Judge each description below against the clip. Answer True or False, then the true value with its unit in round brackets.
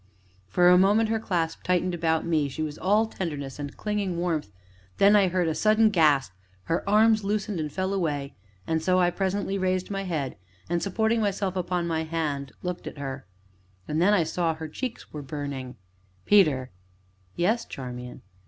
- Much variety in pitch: False (4.4 semitones)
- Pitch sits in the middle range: True (175 Hz)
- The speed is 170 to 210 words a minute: True (180 wpm)